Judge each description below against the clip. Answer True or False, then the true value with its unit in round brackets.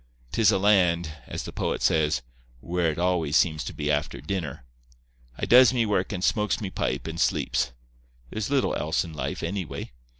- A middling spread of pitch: True (4.7 semitones)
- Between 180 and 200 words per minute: True (185 wpm)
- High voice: False (90 Hz)